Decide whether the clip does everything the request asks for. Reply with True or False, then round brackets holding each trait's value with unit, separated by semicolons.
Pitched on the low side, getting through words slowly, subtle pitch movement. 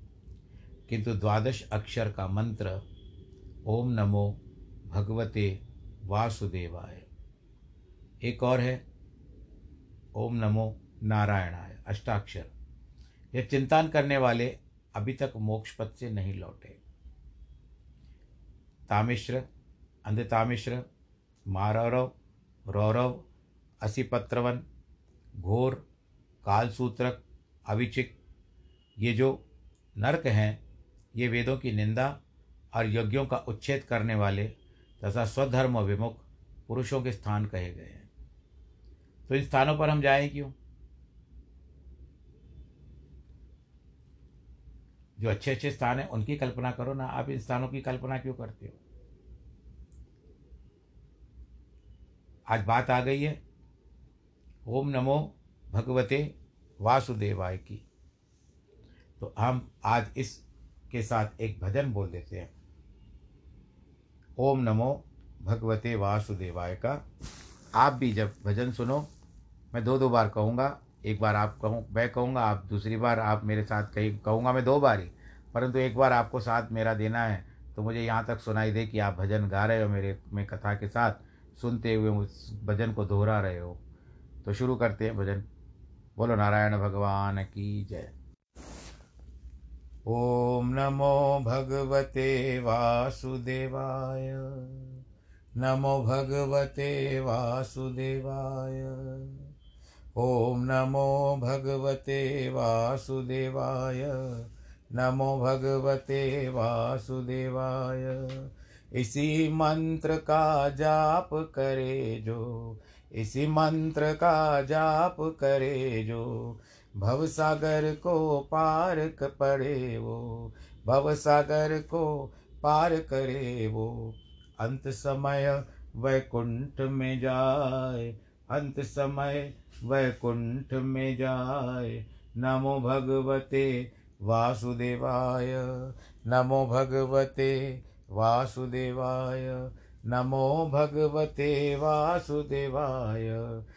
False (115 Hz; 100 wpm; 4.7 semitones)